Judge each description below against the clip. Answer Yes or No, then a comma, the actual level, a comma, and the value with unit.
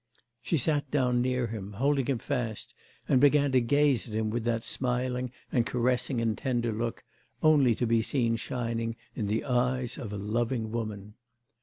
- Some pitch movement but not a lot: No, narrow, 2.2 semitones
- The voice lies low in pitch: Yes, low, 120 Hz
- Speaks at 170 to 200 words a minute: Yes, average, 175 wpm